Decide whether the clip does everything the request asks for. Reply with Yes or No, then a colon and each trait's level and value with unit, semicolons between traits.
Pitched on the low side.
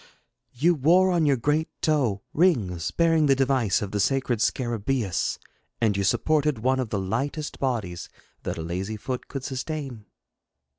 Yes: low, 130 Hz